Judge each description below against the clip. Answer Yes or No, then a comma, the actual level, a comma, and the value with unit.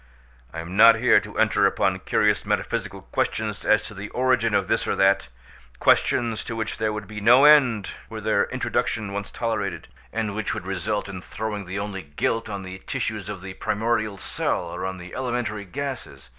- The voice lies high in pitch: No, low, 105 Hz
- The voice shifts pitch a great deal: No, average, 3.1 semitones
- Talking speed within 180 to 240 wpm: Yes, average, 185 wpm